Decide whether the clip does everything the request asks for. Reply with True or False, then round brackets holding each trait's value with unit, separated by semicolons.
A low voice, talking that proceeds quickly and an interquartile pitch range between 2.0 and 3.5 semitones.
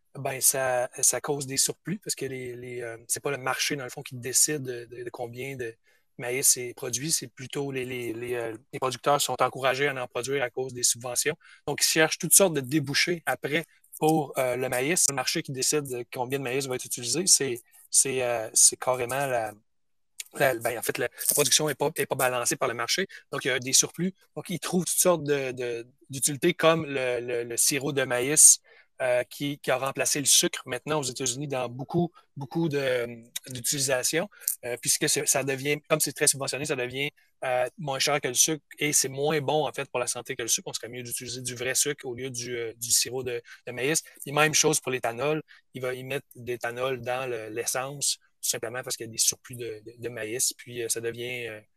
True (130 Hz; 230 wpm; 3.2 semitones)